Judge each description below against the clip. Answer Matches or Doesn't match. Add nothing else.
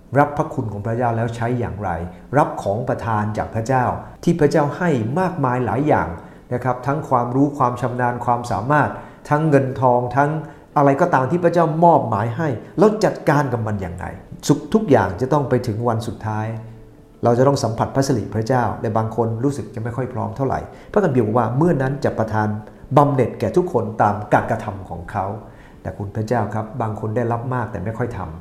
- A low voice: Matches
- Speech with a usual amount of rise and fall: Matches